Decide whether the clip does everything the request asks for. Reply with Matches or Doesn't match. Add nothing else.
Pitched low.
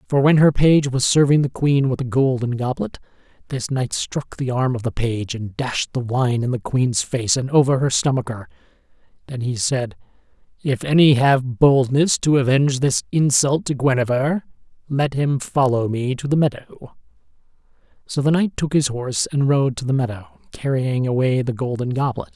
Matches